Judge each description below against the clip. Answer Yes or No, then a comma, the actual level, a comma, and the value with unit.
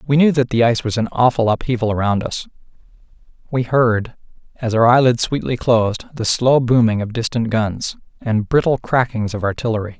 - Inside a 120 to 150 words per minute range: No, average, 175 wpm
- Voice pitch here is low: Yes, low, 120 Hz